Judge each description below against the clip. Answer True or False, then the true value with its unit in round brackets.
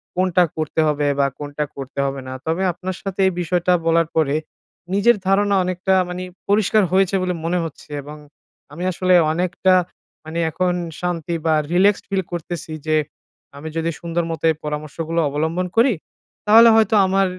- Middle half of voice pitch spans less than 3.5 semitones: True (3.1 semitones)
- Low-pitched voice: False (175 Hz)